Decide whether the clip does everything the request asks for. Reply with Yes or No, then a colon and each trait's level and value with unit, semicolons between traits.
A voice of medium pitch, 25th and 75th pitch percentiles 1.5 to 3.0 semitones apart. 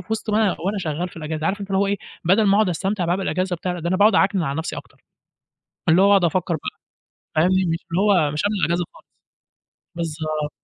No: medium, 180 Hz; average, 3.4 semitones